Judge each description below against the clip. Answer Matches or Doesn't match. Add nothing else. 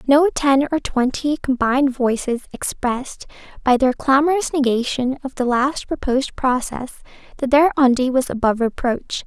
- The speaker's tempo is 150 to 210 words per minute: Doesn't match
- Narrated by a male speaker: Doesn't match